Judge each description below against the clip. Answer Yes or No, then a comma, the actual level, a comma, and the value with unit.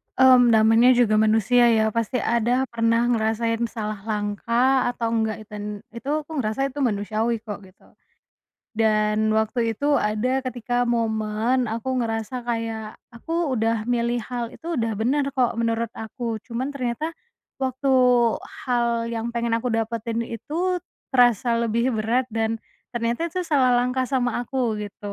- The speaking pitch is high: Yes, high, 235 Hz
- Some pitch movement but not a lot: No, narrow, 2.3 semitones